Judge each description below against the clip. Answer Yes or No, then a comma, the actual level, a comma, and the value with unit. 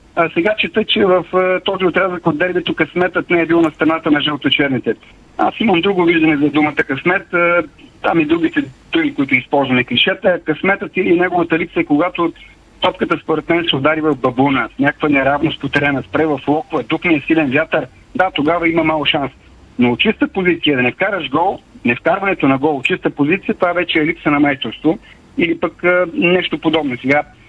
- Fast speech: Yes, fast, 195 wpm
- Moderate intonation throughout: Yes, average, 3.6 semitones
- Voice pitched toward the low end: No, medium, 165 Hz